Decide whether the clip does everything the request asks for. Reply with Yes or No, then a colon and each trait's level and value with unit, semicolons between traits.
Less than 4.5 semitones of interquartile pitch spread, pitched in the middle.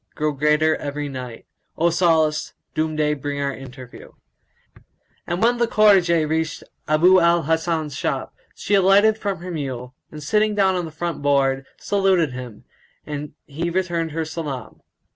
Yes: average, 3.8 semitones; medium, 160 Hz